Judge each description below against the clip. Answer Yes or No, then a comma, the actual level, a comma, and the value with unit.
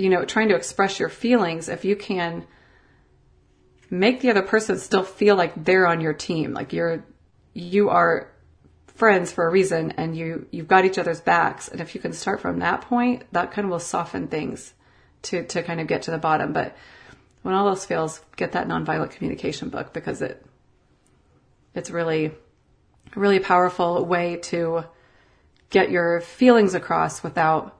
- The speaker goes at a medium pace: Yes, average, 175 wpm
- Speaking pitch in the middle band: Yes, medium, 175 Hz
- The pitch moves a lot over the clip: No, average, 3.2 semitones